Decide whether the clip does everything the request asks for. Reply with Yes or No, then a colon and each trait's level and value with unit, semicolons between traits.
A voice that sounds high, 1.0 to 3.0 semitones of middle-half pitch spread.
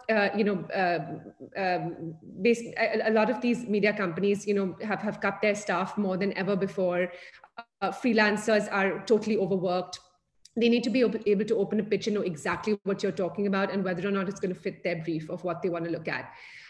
Yes: high, 200 Hz; average, 2.7 semitones